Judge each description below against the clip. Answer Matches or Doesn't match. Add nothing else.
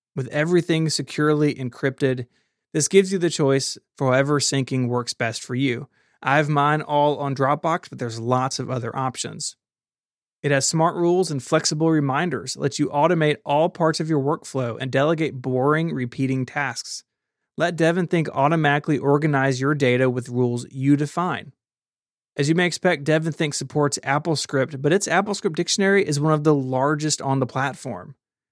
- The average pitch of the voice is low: Doesn't match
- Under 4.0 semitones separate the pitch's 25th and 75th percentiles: Matches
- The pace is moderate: Matches